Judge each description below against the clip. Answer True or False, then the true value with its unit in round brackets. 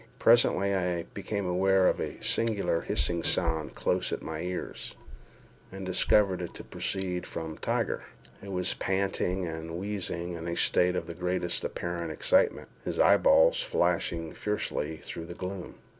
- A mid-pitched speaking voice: False (90 Hz)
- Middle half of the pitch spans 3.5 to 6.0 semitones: False (2.5 semitones)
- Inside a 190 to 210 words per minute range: False (150 wpm)